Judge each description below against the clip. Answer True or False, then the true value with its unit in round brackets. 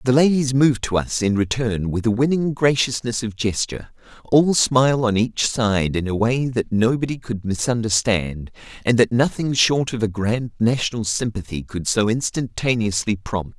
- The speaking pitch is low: True (115 Hz)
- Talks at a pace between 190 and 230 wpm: False (170 wpm)